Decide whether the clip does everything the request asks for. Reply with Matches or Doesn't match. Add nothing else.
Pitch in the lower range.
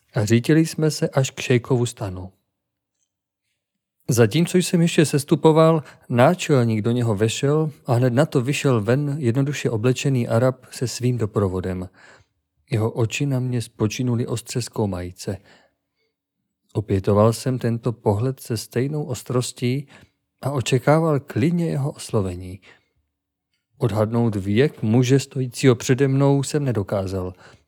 Matches